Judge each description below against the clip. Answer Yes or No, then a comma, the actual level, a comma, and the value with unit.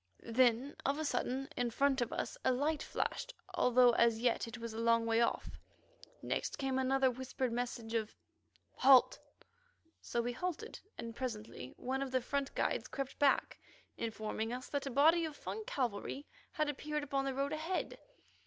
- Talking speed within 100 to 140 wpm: No, average, 170 wpm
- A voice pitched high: Yes, very high, 260 Hz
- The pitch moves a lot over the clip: No, average, 3.2 semitones